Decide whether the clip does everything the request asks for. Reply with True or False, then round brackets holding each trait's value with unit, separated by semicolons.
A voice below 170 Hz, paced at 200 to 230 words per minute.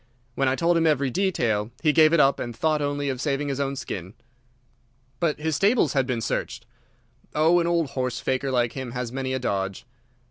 True (135 Hz; 205 wpm)